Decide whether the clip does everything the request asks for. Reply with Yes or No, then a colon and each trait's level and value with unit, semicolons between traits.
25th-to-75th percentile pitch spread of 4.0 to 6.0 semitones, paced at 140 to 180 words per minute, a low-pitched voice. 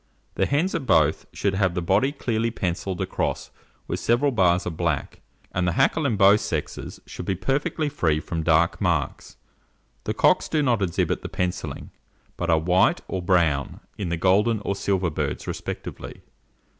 Yes: average, 5.0 semitones; average, 170 wpm; very low, 95 Hz